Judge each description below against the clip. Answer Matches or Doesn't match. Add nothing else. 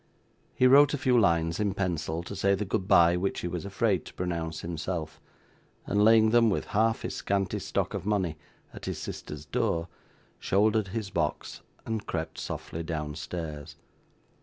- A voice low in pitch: Matches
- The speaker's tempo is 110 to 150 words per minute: Doesn't match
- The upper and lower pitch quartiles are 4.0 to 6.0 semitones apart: Matches